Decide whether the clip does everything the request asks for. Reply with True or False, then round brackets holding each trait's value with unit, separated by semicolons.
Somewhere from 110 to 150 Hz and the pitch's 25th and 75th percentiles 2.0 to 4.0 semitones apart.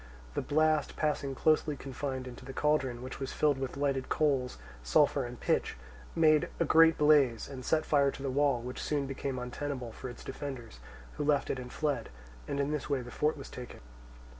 True (140 Hz; 2.6 semitones)